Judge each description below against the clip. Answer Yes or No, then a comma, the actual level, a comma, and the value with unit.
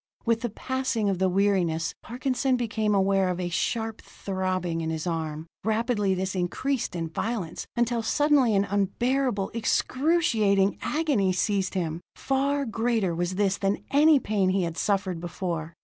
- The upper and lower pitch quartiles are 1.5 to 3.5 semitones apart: No, average, 4.6 semitones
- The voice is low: No, high, 200 Hz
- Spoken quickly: No, average, 150 wpm